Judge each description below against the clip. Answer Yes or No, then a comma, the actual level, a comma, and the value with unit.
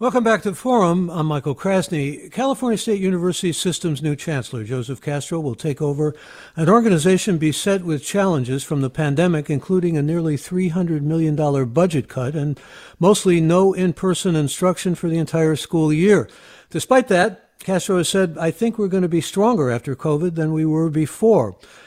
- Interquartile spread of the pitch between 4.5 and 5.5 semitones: No, average, 3.9 semitones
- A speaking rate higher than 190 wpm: No, average, 170 wpm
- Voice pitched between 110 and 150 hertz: No, medium, 170 Hz